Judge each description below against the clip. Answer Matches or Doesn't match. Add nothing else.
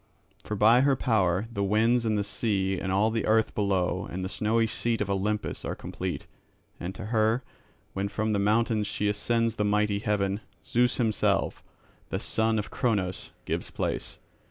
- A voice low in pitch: Matches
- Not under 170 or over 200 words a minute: Matches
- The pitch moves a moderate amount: Doesn't match